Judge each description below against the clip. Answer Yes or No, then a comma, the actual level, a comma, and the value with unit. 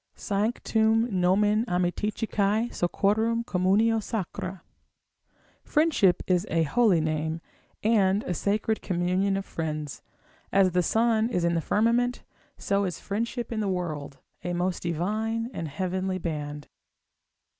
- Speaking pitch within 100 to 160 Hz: No, high, 195 Hz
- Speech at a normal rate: No, slow, 125 wpm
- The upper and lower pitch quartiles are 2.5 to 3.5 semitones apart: No, average, 3.9 semitones